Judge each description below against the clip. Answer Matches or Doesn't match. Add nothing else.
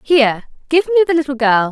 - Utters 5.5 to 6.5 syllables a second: Doesn't match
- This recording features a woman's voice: Matches